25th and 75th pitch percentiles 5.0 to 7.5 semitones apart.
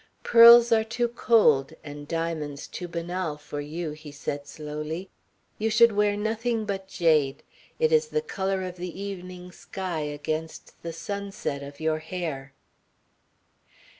Yes: wide, 5.4 semitones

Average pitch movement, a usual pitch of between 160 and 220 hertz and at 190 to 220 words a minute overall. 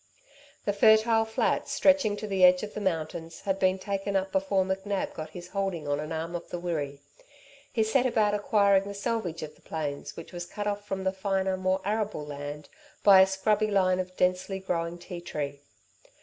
Yes: average, 3.0 semitones; high, 190 Hz; average, 195 wpm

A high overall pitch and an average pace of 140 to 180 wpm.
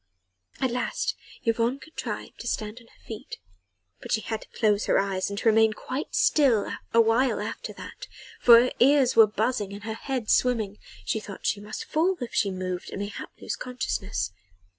No: high, 225 Hz; average, 190 wpm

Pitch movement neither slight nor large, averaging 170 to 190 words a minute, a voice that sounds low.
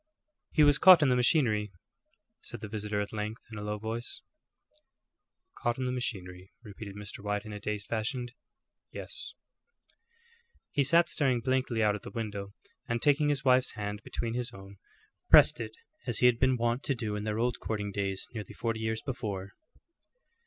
Yes: average, 3.5 semitones; average, 180 wpm; low, 110 Hz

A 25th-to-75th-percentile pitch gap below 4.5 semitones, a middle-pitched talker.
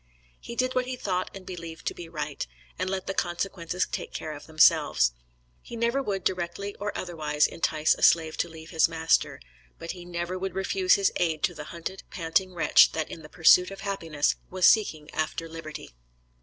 Yes: average, 3.0 semitones; medium, 175 Hz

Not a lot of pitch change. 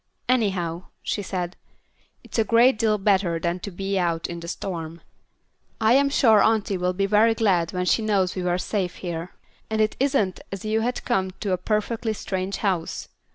No: average, 3.5 semitones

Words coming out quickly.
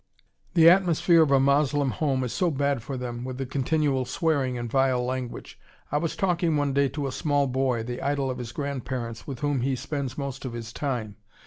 Yes: fast, 210 wpm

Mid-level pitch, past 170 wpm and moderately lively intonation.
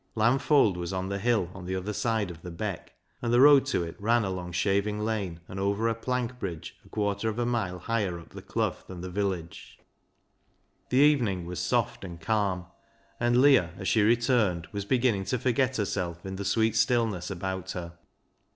No: low, 100 Hz; average, 195 wpm; average, 4.4 semitones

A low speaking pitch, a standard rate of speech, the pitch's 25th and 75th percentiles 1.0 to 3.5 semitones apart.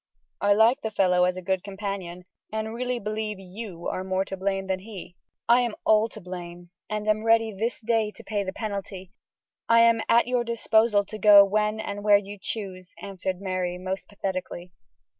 No: high, 205 Hz; average, 190 wpm; average, 2.7 semitones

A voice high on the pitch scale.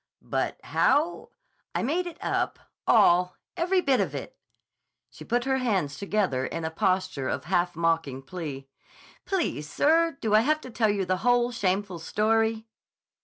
Yes: high, 205 Hz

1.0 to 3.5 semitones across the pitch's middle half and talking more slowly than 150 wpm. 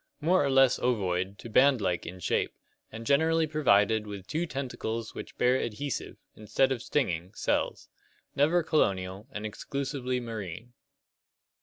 No: wide, 5.5 semitones; average, 140 wpm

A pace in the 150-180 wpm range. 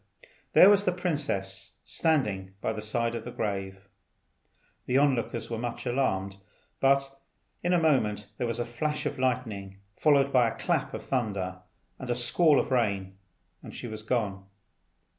Yes: average, 165 wpm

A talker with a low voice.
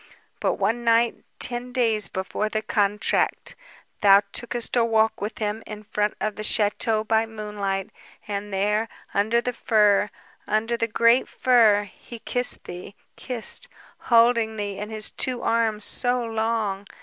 No: high, 220 Hz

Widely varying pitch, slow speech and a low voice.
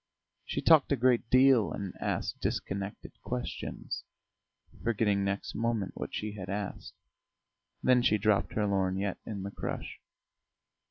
No: average, 3.0 semitones; slow, 130 wpm; low, 105 Hz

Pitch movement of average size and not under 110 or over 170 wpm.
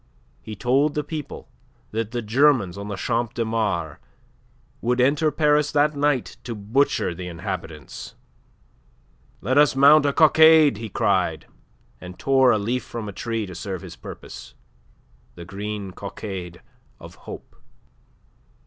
No: wide, 6.1 semitones; average, 140 wpm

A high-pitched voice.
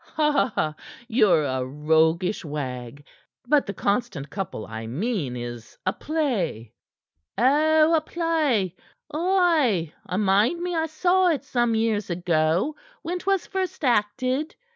Yes: high, 215 Hz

